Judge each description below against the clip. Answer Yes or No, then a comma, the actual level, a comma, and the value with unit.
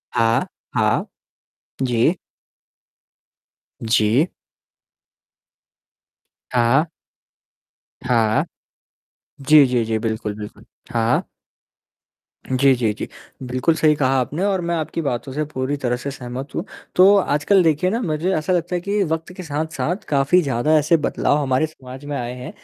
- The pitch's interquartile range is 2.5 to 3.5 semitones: No, average, 4.6 semitones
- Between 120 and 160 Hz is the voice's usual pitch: Yes, medium, 140 Hz